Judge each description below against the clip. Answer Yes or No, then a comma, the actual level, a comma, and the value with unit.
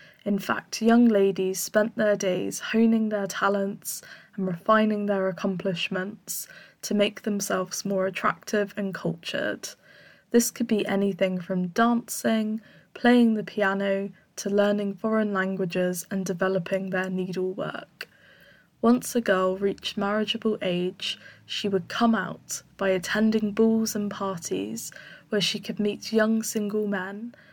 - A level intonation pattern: Yes, narrow, 2.3 semitones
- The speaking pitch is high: Yes, high, 200 Hz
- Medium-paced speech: No, slow, 130 wpm